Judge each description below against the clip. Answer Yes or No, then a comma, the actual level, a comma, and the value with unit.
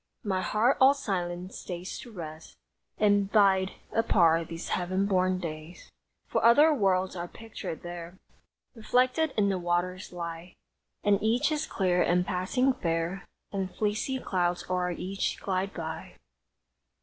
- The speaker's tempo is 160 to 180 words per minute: No, slow, 135 wpm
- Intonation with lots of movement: No, average, 3.4 semitones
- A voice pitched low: No, medium, 185 Hz